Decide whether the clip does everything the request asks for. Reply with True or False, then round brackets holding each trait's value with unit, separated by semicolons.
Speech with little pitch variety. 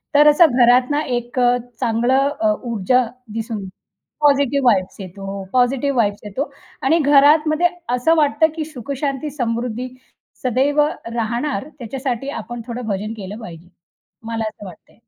False (4.0 semitones)